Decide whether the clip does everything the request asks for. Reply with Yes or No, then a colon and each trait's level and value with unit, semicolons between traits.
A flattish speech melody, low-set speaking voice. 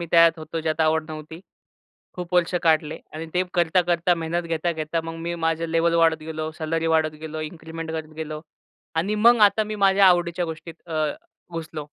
No: narrow, 1.4 semitones; medium, 165 Hz